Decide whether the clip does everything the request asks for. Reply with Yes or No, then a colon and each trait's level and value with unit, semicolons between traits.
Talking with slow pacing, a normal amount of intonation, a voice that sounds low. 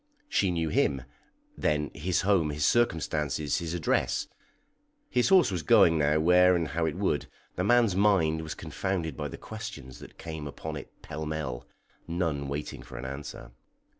No: average, 165 wpm; average, 3.6 semitones; very low, 80 Hz